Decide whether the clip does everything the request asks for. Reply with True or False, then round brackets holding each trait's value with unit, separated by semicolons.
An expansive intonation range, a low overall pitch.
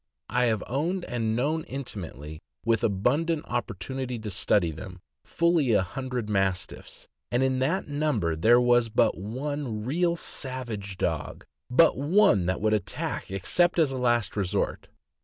True (5.9 semitones; 120 Hz)